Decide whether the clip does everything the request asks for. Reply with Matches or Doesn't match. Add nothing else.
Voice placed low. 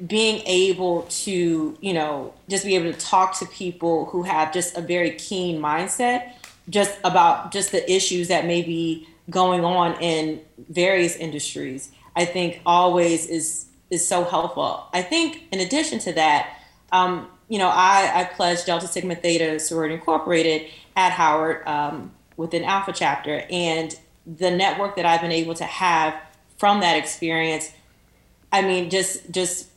Doesn't match